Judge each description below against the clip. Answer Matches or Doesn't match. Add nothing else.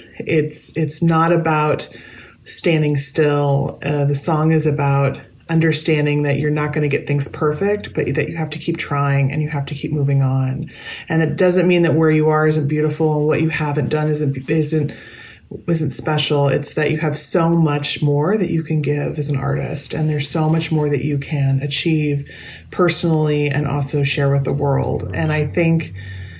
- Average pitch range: Doesn't match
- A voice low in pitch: Doesn't match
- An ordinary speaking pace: Matches